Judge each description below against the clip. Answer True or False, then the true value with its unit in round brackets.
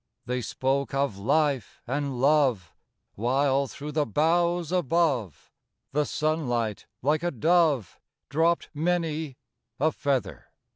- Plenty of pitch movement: False (3.7 semitones)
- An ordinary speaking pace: False (110 wpm)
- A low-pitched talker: False (145 Hz)